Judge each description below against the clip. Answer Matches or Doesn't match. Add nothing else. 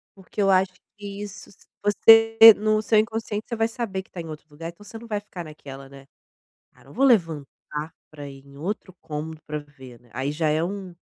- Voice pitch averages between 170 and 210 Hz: Matches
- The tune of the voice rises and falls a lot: Matches